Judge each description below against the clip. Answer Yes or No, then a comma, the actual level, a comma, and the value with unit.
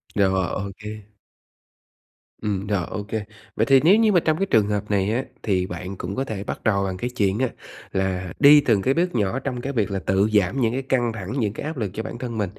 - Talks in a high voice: No, low, 105 Hz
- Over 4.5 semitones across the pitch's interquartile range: Yes, average, 4.9 semitones